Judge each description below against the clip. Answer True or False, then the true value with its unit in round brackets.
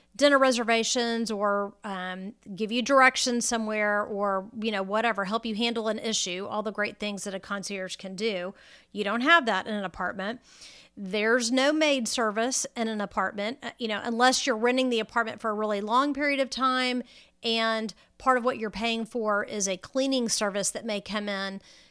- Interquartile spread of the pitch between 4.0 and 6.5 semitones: False (3.2 semitones)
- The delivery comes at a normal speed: True (190 wpm)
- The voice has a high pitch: True (220 Hz)